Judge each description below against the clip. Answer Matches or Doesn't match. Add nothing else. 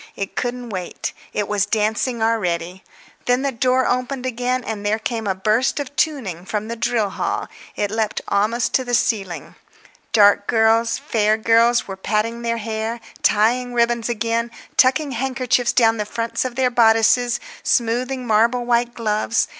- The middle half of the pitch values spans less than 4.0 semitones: Matches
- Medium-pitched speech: Doesn't match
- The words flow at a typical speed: Matches